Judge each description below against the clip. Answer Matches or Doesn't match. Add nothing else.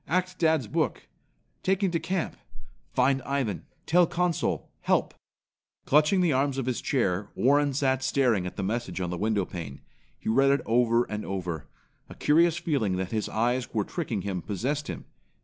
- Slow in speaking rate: Doesn't match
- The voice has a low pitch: Matches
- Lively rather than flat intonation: Matches